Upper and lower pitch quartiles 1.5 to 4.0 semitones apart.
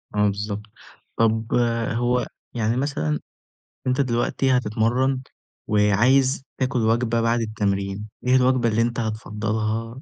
Yes: average, 2.9 semitones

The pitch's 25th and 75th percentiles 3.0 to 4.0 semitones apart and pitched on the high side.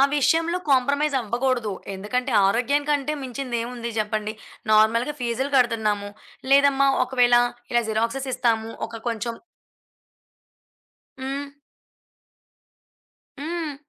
Yes: average, 3.4 semitones; very high, 250 Hz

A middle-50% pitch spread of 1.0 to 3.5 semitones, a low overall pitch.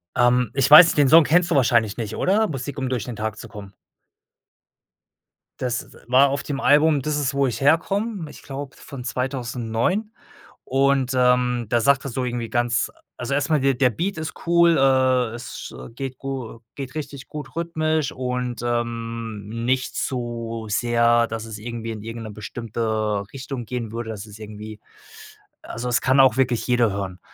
Yes: average, 3.1 semitones; low, 125 Hz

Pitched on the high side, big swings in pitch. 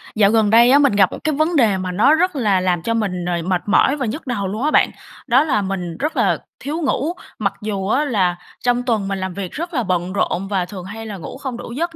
Yes: high, 215 Hz; wide, 6.0 semitones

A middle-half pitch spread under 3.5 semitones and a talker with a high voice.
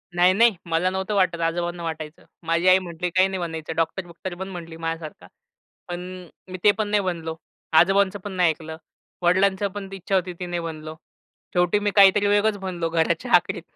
No: narrow, 2.6 semitones; medium, 180 Hz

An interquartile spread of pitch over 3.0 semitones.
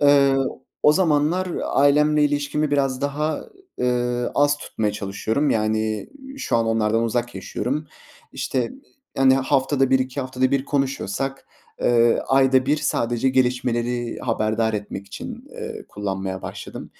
Yes: average, 3.7 semitones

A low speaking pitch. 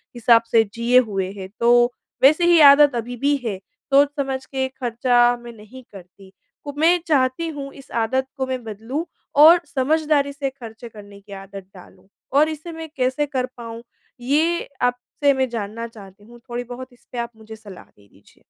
No: high, 245 Hz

